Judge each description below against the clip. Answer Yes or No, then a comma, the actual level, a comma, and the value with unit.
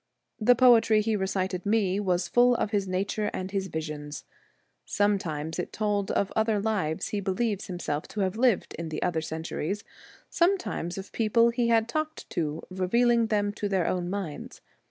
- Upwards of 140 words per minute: Yes, average, 165 wpm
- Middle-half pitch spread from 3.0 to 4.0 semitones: Yes, average, 3.7 semitones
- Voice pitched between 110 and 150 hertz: No, high, 200 Hz